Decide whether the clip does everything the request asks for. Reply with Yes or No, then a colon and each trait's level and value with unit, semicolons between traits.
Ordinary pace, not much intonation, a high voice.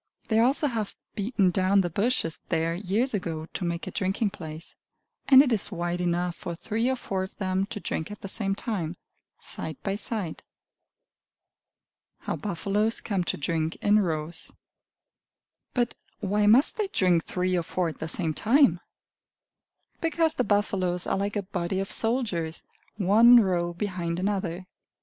No: average, 160 wpm; average, 3.9 semitones; high, 195 Hz